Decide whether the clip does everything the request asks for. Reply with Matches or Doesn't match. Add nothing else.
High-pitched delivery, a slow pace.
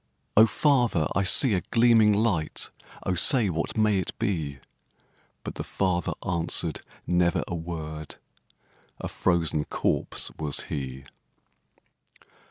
Doesn't match